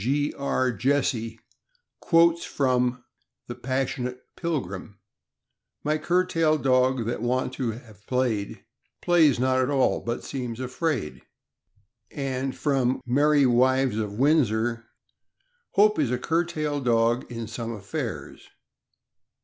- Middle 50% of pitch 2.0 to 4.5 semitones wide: Yes, average, 3.5 semitones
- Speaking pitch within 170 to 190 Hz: No, low, 130 Hz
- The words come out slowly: Yes, slow, 125 wpm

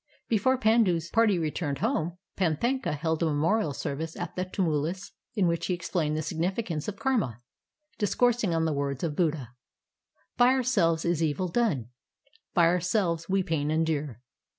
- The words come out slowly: No, average, 155 wpm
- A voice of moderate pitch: Yes, medium, 170 Hz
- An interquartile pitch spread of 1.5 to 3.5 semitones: No, average, 4.7 semitones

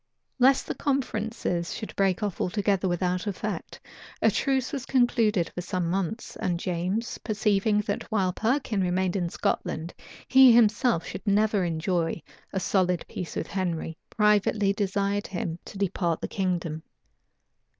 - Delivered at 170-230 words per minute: No, average, 140 wpm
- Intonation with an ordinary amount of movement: Yes, average, 3.4 semitones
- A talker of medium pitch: No, high, 195 Hz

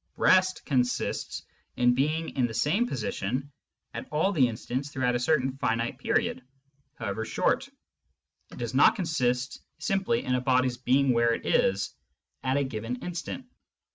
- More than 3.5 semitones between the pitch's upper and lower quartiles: Yes, average, 4.3 semitones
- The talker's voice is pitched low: Yes, low, 130 Hz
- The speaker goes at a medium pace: Yes, average, 150 wpm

